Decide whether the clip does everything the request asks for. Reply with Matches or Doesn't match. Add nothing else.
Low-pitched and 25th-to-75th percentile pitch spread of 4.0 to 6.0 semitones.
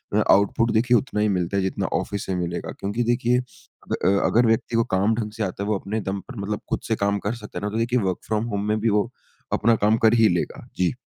Doesn't match